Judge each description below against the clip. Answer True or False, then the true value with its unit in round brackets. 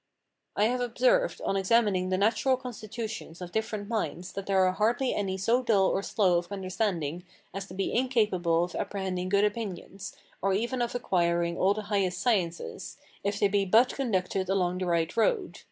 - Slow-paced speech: False (180 wpm)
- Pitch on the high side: True (200 Hz)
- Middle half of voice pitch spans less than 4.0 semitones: True (3.5 semitones)